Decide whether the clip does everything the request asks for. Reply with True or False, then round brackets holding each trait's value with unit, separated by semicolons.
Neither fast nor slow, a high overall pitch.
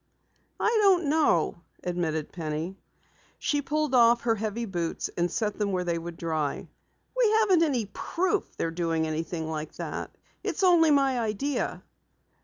True (150 wpm; 210 Hz)